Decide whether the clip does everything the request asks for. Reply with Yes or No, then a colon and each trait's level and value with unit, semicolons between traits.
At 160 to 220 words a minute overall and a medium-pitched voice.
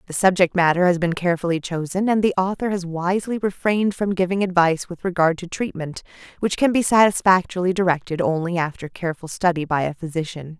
Yes: average, 180 wpm; medium, 180 Hz